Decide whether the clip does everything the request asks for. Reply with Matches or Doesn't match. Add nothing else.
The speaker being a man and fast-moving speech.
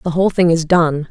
Doesn't match